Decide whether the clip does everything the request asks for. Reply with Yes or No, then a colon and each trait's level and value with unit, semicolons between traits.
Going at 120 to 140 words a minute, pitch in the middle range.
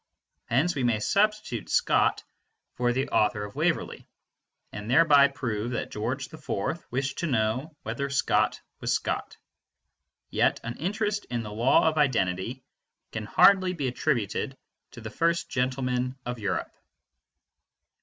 No: slow, 135 wpm; low, 130 Hz